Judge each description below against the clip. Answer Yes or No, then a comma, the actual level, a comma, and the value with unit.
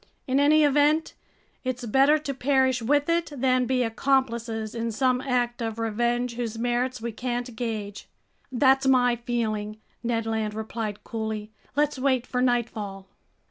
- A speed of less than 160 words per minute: Yes, average, 145 wpm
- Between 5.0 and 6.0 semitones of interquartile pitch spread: No, average, 2.8 semitones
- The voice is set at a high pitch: Yes, high, 245 Hz